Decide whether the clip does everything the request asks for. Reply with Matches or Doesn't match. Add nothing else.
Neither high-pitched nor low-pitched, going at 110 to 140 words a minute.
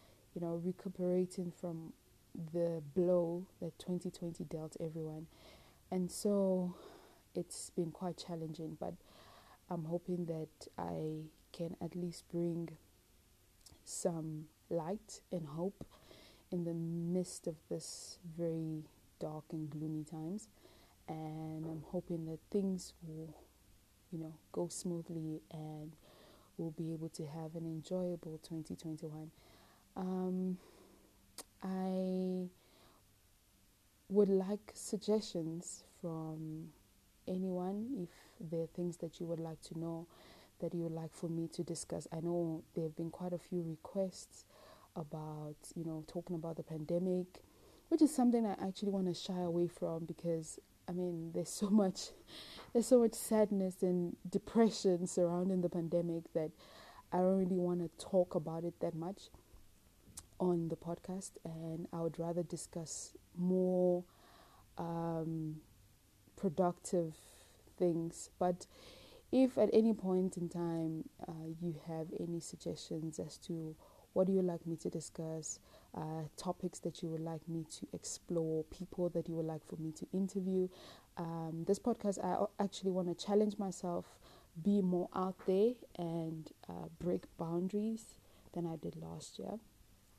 Matches